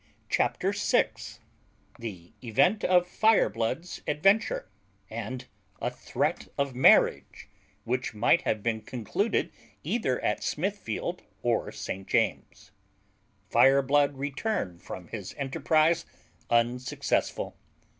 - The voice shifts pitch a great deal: Yes, wide, 6.6 semitones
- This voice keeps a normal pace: No, slow, 95 wpm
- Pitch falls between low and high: No, low, 130 Hz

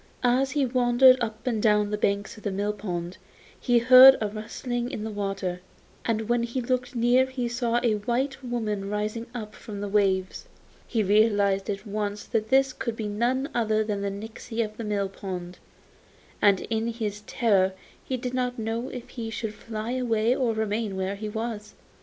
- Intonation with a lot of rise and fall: No, average, 2.8 semitones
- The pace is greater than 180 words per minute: Yes, average, 190 wpm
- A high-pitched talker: Yes, high, 220 Hz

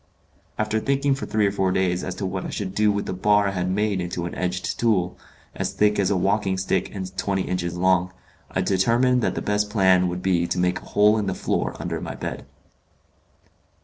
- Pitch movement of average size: No, narrow, 2.3 semitones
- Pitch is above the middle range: No, very low, 95 Hz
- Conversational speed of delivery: No, fast, 220 wpm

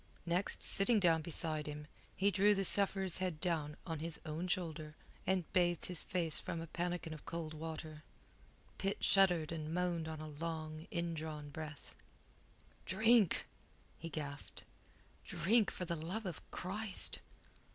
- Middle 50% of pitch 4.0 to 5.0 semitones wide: No, average, 3.0 semitones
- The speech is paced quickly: No, average, 145 wpm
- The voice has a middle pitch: Yes, medium, 170 Hz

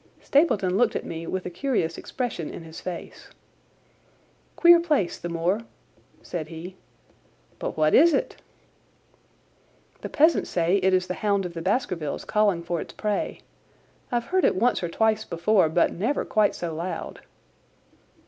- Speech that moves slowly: No, average, 155 wpm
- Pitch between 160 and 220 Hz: Yes, medium, 185 Hz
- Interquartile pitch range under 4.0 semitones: No, average, 4.7 semitones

